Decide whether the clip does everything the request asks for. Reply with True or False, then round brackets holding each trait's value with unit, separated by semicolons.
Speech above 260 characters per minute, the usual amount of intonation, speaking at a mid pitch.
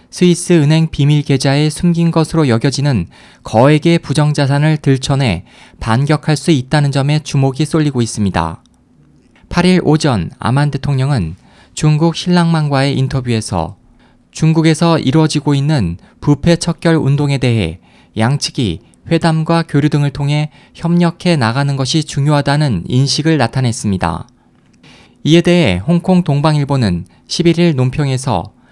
True (295 characters per minute; 4.0 semitones; 145 Hz)